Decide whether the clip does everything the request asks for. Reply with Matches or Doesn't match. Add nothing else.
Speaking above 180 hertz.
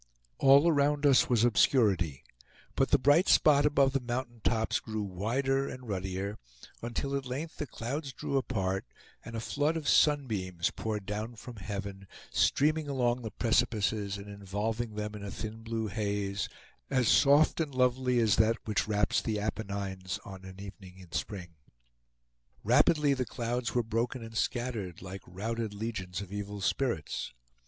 Doesn't match